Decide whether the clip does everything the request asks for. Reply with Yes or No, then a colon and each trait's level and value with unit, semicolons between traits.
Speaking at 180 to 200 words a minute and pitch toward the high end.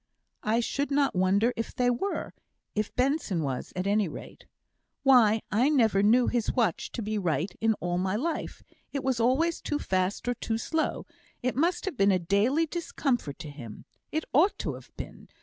Yes: average, 185 wpm; high, 230 Hz